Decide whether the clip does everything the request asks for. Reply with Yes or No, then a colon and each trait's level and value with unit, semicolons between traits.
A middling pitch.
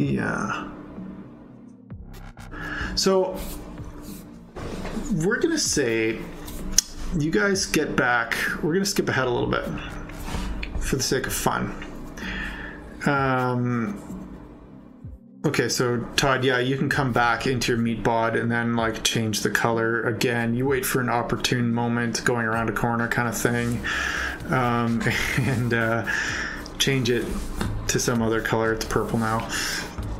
No: low, 120 Hz